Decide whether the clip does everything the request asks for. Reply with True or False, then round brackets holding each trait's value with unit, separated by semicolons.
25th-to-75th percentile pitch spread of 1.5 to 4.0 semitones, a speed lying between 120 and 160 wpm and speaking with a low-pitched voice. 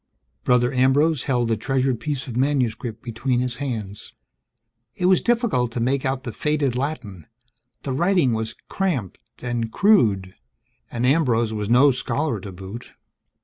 True (3.7 semitones; 145 wpm; 125 Hz)